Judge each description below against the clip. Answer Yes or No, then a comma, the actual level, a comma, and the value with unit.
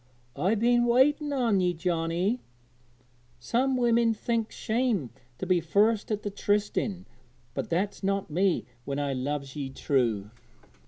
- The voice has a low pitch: No, high, 200 Hz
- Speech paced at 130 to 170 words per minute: Yes, average, 140 wpm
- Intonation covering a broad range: Yes, wide, 6.7 semitones